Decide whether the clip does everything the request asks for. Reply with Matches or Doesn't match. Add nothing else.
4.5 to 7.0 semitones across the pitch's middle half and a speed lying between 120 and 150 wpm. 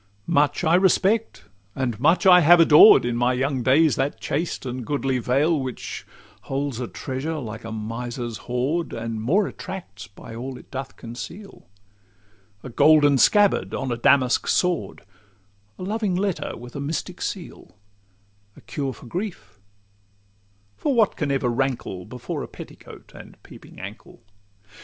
Matches